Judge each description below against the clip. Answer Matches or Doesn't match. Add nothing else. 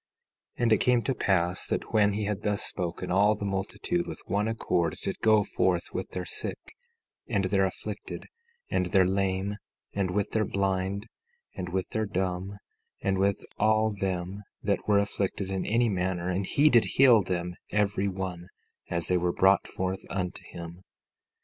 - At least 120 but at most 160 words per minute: Doesn't match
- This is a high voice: Doesn't match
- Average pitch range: Doesn't match